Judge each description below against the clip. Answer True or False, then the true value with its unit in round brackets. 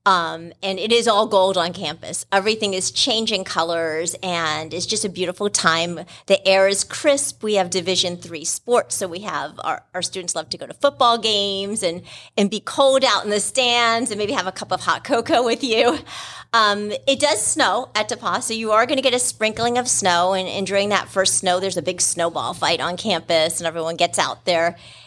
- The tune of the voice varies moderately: True (4.2 semitones)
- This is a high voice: True (195 Hz)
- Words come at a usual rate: False (220 wpm)